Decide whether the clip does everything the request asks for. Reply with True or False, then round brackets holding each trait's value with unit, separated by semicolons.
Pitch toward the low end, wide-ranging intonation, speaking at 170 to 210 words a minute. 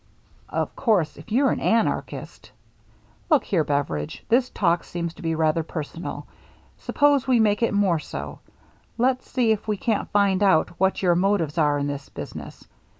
False (190 Hz; 5.8 semitones; 190 wpm)